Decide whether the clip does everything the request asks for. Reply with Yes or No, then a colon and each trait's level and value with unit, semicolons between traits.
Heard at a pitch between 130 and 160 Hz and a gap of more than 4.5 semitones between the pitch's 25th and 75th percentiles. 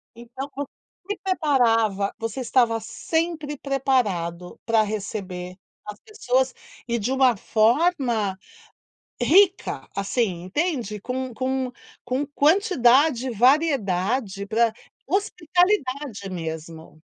No: high, 245 Hz; wide, 5.6 semitones